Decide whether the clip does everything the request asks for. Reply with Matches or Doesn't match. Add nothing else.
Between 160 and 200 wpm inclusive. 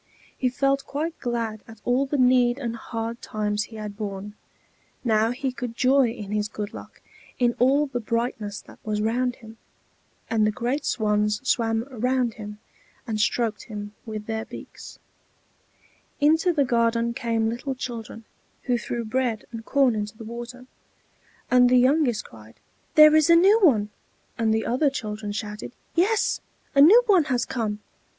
Matches